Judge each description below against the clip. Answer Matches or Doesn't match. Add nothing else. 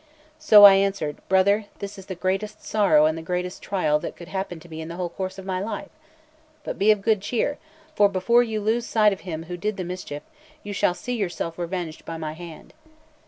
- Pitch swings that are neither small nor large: Matches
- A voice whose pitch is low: Doesn't match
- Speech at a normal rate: Doesn't match